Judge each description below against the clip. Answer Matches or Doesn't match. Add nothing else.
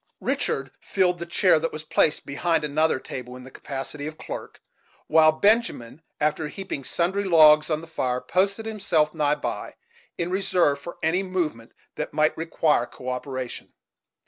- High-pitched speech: Doesn't match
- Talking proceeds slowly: Doesn't match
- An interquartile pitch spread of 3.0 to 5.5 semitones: Matches